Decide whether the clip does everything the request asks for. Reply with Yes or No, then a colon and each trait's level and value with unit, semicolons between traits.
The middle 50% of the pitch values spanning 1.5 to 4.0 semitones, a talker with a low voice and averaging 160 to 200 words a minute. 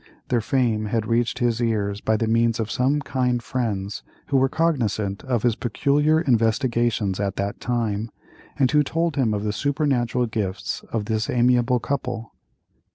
Yes: average, 3.1 semitones; low, 120 Hz; average, 165 wpm